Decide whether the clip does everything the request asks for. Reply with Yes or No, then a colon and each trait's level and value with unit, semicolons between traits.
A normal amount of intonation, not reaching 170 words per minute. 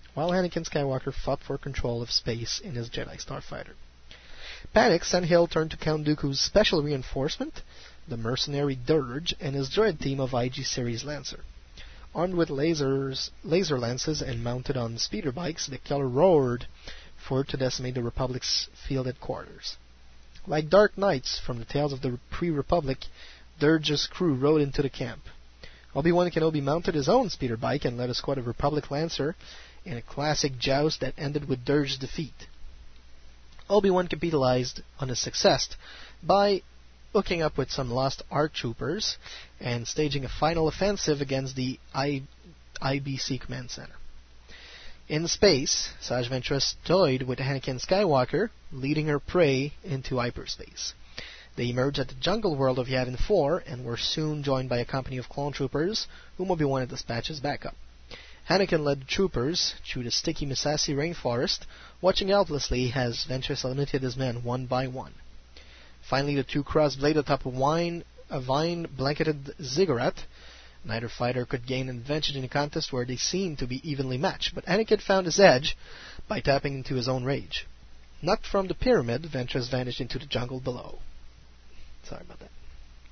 Yes: average, 3.8 semitones; average, 160 wpm